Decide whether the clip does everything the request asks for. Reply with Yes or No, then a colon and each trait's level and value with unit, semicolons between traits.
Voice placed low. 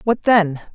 No: high, 200 Hz